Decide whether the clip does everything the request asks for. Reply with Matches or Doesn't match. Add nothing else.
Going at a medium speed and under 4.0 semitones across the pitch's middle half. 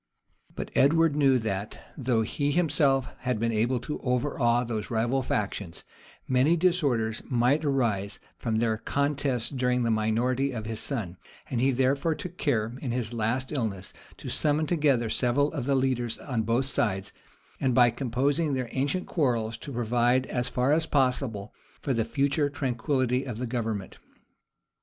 Matches